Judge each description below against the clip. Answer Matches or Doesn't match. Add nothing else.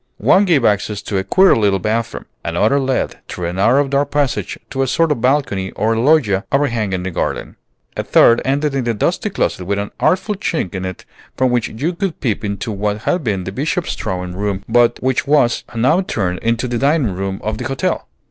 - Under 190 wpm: Doesn't match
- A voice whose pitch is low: Matches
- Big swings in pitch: Matches